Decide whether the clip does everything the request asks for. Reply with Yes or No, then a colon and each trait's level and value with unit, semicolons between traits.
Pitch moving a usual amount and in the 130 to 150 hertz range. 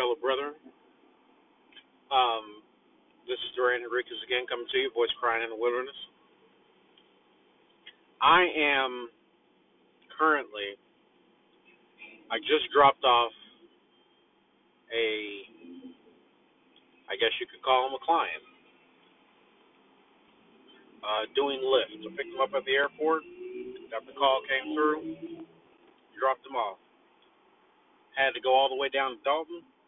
No: wide, 6.0 semitones; low, 135 Hz